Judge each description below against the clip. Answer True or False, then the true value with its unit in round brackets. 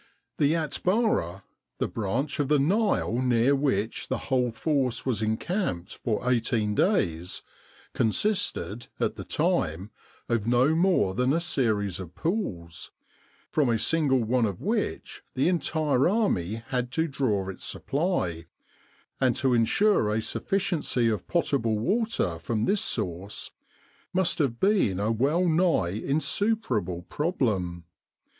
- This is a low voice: True (125 Hz)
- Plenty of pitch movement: True (7.5 semitones)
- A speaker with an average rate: False (130 wpm)